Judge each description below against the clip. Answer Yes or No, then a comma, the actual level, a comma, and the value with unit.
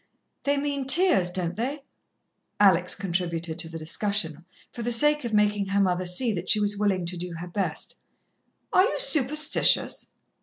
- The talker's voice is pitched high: Yes, high, 200 Hz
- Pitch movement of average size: No, wide, 6.0 semitones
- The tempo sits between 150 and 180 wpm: Yes, average, 165 wpm